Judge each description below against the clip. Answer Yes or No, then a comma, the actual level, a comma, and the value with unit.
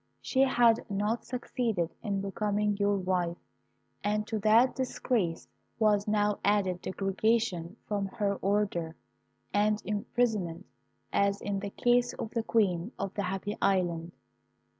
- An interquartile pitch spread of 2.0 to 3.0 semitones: Yes, narrow, 2.4 semitones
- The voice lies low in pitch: No, high, 205 Hz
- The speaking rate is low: Yes, slow, 130 wpm